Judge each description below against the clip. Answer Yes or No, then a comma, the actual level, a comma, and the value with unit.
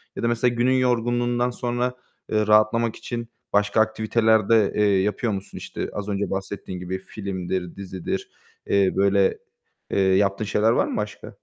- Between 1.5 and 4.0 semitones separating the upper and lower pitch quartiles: Yes, average, 3.1 semitones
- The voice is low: Yes, low, 105 Hz